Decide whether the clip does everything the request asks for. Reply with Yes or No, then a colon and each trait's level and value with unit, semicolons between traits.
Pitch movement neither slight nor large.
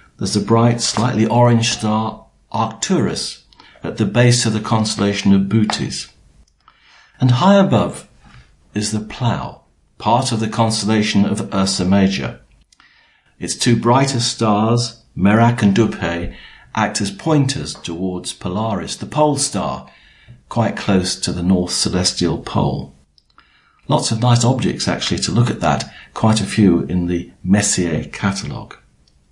Yes: average, 4.1 semitones